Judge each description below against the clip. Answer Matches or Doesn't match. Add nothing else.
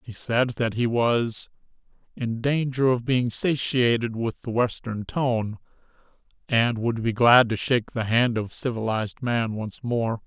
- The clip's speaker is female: Doesn't match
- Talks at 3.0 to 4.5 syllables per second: Matches